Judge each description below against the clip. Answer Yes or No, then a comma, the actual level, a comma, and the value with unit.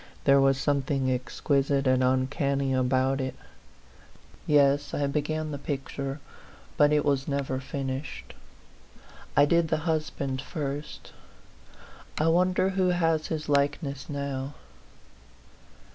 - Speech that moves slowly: Yes, slow, 115 wpm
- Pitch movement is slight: Yes, narrow, 2.0 semitones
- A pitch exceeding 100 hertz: Yes, medium, 140 Hz